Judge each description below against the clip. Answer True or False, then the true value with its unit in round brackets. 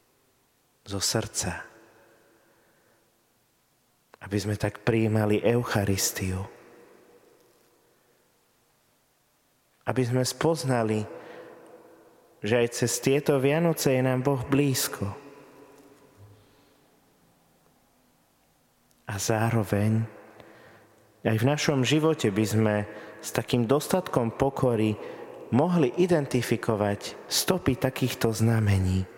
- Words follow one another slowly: True (75 wpm)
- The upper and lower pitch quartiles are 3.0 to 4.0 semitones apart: False (4.6 semitones)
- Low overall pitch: True (120 Hz)